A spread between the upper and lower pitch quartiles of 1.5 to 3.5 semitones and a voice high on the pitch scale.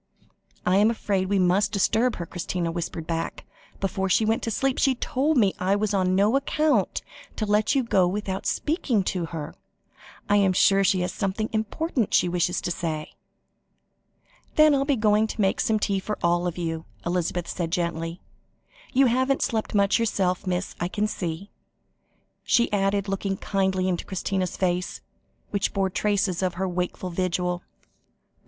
Yes: average, 3.2 semitones; high, 195 Hz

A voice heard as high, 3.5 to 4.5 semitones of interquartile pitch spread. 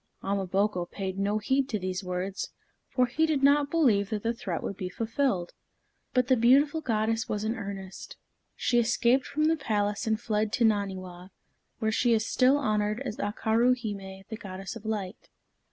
Yes: high, 215 Hz; average, 4.0 semitones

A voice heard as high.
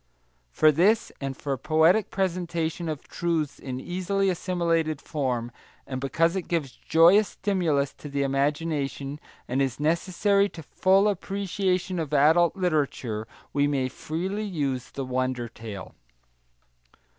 No: medium, 160 Hz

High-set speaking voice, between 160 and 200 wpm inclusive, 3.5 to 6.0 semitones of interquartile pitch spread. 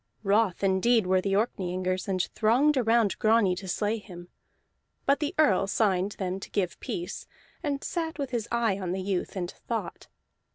Yes: high, 200 Hz; average, 170 wpm; average, 3.9 semitones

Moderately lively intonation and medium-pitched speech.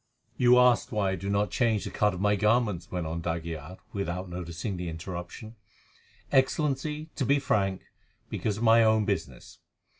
No: average, 4.9 semitones; low, 105 Hz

